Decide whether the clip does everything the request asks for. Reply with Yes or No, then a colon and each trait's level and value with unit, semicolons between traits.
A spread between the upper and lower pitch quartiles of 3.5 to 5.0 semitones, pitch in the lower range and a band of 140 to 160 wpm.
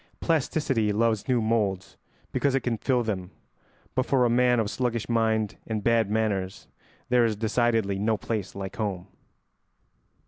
No: average, 2.8 semitones; low, 110 Hz; average, 150 wpm